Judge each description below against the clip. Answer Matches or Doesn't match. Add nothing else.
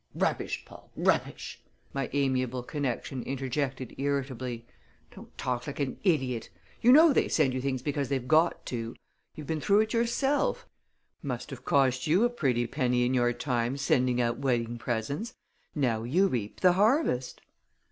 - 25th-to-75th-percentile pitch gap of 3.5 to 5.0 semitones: Matches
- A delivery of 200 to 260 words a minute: Doesn't match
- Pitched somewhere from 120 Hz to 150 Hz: Matches